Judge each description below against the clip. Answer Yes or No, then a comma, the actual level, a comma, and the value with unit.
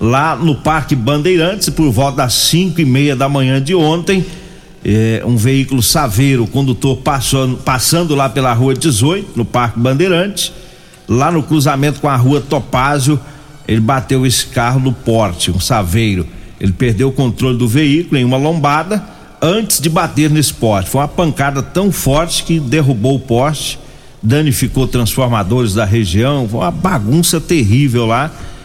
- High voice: No, low, 135 Hz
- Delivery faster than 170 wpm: No, average, 160 wpm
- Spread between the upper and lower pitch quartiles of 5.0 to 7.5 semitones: No, average, 4.3 semitones